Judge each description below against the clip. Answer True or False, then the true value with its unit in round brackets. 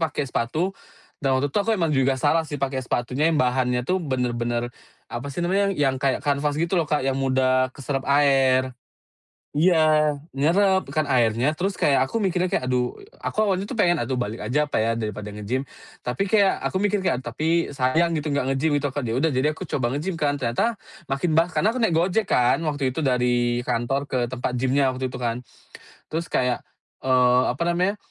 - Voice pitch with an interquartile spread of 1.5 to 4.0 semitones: False (4.4 semitones)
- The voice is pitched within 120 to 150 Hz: True (140 Hz)